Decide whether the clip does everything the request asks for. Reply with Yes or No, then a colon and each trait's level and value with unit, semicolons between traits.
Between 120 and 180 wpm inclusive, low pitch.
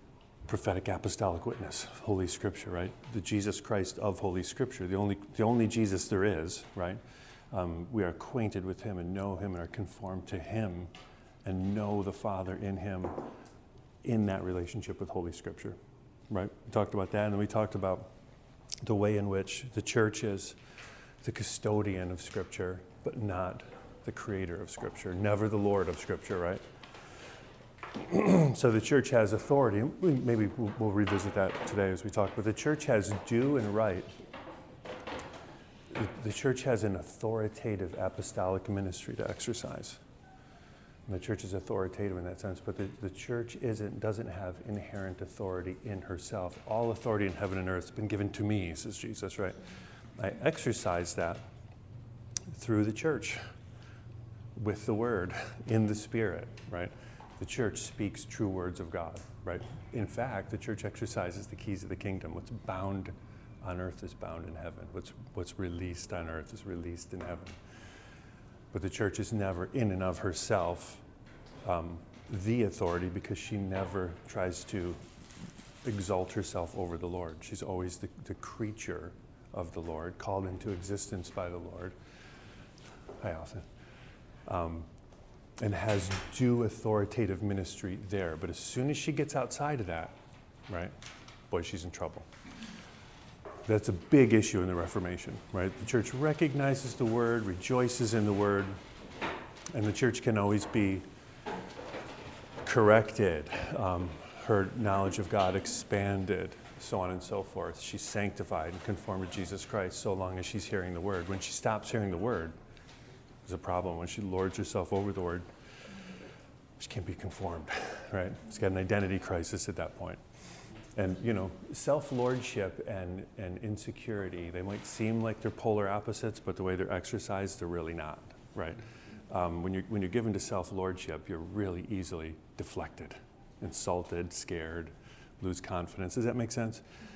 Yes: average, 160 wpm; low, 100 Hz